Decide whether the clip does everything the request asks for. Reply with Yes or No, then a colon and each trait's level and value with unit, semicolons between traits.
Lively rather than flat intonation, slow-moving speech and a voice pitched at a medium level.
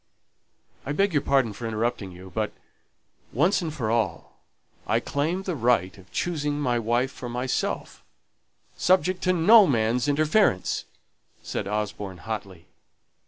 No: wide, 6.5 semitones; slow, 130 wpm; low, 125 Hz